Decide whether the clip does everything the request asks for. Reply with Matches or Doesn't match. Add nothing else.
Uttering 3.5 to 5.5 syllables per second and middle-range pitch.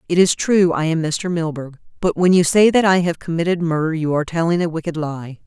Doesn't match